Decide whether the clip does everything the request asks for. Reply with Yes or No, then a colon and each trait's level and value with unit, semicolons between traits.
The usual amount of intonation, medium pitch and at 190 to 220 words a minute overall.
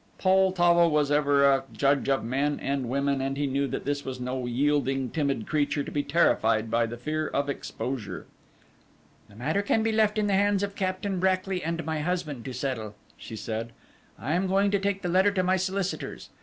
No: wide, 5.7 semitones; medium, 145 Hz; average, 200 wpm